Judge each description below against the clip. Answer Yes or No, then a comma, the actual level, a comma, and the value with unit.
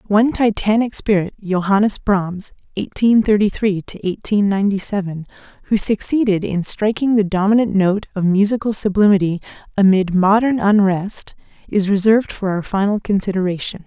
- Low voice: No, high, 200 Hz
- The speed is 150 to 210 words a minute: No, slow, 135 wpm